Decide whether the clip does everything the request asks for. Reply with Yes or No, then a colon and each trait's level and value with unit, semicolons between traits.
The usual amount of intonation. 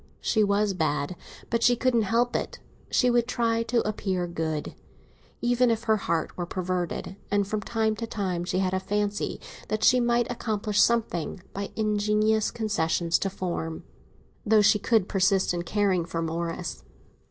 Yes: average, 3.8 semitones